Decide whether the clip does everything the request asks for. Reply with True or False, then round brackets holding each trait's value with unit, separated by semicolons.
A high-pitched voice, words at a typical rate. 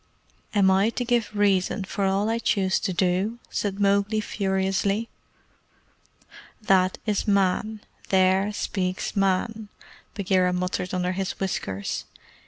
False (195 Hz; 120 wpm)